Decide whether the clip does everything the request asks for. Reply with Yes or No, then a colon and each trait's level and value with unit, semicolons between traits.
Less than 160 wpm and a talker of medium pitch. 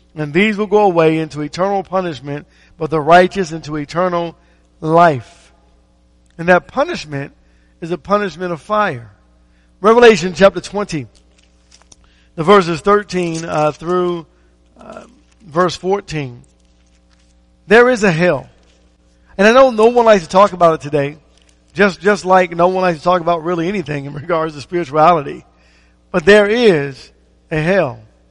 Yes: average, 145 wpm; medium, 165 Hz